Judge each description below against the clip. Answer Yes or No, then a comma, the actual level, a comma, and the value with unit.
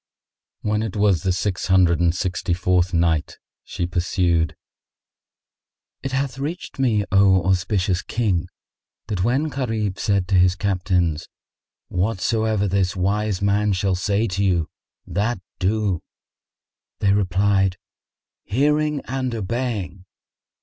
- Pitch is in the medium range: No, low, 100 Hz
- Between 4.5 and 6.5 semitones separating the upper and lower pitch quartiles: No, average, 3.1 semitones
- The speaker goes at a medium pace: No, slow, 120 wpm